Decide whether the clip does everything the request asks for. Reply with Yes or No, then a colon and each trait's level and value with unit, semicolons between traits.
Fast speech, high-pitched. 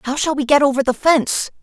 Yes: fast, 260 wpm; very high, 275 Hz